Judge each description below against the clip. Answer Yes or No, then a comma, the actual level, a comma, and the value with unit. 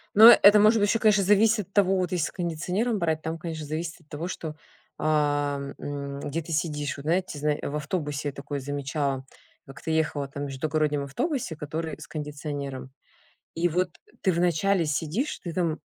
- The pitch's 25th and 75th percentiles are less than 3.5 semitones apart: No, average, 3.8 semitones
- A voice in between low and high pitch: Yes, medium, 155 Hz